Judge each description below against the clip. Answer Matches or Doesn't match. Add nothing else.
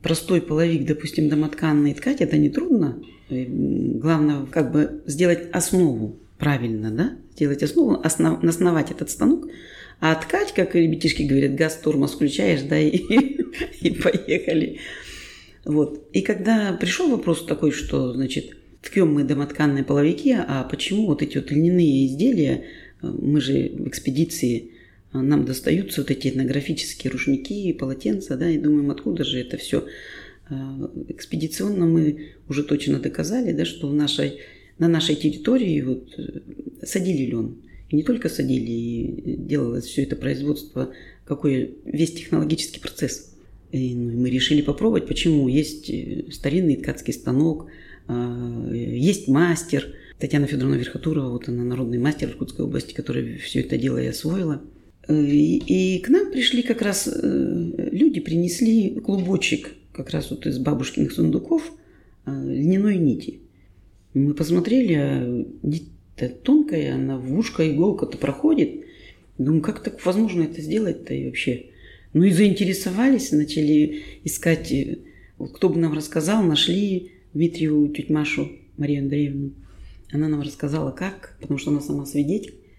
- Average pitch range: Matches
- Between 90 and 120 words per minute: Doesn't match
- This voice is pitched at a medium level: Matches